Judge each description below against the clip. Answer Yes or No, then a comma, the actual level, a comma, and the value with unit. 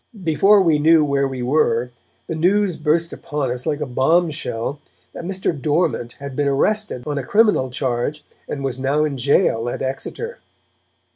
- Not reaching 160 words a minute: No, average, 170 wpm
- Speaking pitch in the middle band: Yes, medium, 145 Hz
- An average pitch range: Yes, average, 4.1 semitones